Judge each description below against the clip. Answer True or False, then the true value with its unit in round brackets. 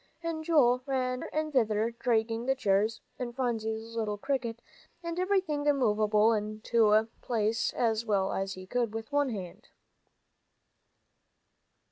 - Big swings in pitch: False (3.7 semitones)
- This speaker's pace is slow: True (130 wpm)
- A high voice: True (230 Hz)